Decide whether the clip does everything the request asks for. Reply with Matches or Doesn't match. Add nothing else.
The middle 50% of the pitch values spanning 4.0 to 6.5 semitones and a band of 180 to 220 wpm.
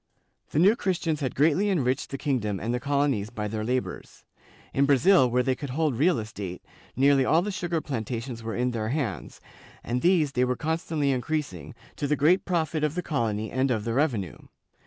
Matches